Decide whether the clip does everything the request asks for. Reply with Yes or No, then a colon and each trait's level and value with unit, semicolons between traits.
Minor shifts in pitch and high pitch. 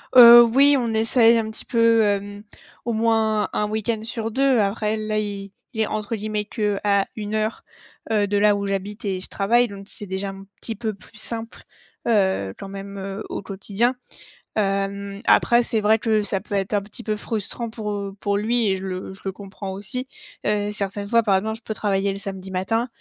Yes: narrow, 2.1 semitones; high, 210 Hz